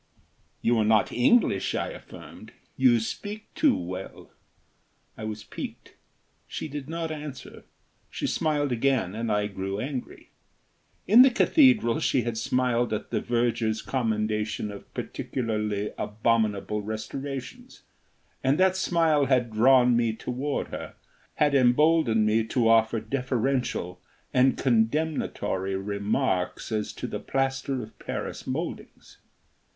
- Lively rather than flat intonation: No, average, 4.2 semitones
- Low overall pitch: Yes, low, 120 Hz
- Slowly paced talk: Yes, slow, 125 wpm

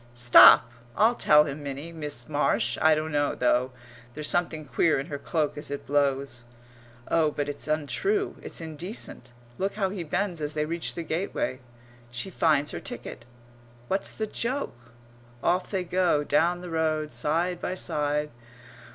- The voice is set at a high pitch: No, medium, 155 Hz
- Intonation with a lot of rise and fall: No, average, 3.4 semitones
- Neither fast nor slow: Yes, average, 160 wpm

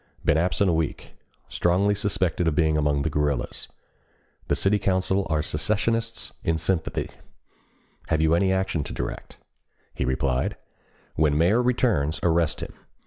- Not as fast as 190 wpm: Yes, average, 140 wpm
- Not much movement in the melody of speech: No, average, 4.1 semitones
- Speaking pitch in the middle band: No, very low, 85 Hz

